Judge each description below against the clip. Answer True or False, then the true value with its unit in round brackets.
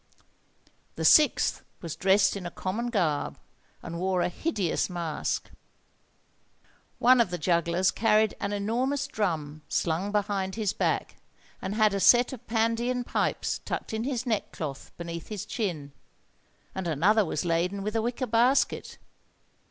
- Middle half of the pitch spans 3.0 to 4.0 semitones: False (4.7 semitones)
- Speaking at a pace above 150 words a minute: False (145 wpm)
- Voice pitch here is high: True (200 Hz)